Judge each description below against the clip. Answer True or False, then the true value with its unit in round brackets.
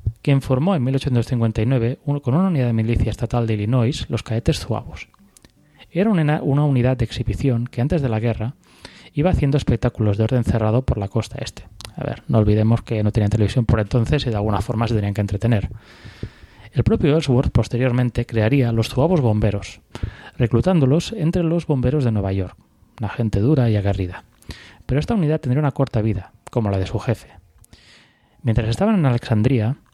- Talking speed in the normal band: True (180 wpm)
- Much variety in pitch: False (3.9 semitones)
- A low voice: True (120 Hz)